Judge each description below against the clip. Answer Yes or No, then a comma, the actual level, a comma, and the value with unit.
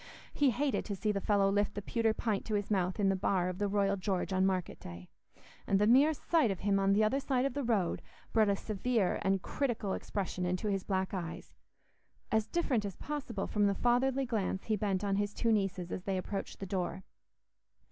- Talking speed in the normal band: No, fast, 220 wpm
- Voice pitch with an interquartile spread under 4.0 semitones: Yes, average, 2.9 semitones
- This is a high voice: Yes, high, 205 Hz